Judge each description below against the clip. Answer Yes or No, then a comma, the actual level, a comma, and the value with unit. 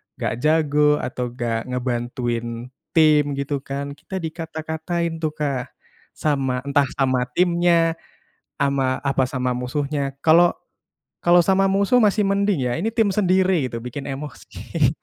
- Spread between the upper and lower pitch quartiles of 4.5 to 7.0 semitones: Yes, average, 4.8 semitones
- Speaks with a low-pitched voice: No, medium, 145 Hz